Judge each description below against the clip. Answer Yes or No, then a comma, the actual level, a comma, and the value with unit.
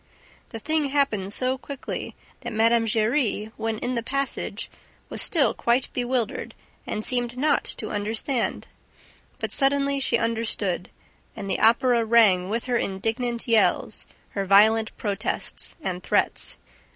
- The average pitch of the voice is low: No, high, 230 Hz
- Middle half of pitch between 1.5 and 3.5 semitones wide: Yes, average, 2.9 semitones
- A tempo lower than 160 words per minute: Yes, slow, 135 wpm